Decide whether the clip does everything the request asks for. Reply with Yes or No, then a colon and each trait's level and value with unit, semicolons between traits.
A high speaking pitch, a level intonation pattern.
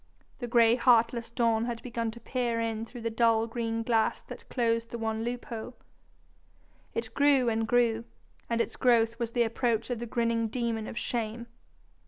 Yes: high, 230 Hz; narrow, 1.1 semitones